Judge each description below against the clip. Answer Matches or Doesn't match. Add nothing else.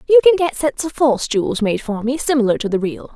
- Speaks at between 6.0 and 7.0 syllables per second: Matches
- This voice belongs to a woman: Matches